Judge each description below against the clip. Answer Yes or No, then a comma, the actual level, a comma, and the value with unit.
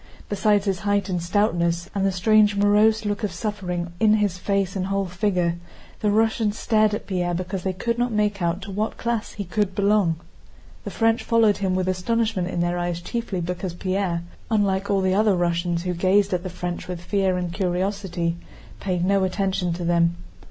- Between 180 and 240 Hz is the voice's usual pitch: Yes, high, 190 Hz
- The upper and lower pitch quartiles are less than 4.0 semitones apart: Yes, average, 2.8 semitones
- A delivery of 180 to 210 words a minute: Yes, average, 195 wpm